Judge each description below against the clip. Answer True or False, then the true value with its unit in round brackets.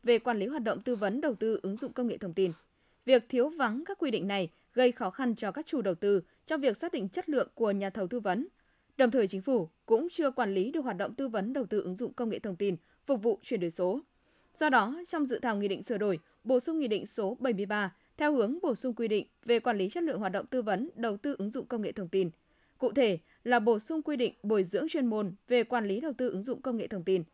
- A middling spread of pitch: True (4.9 semitones)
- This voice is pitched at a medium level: False (235 Hz)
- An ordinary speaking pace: False (280 wpm)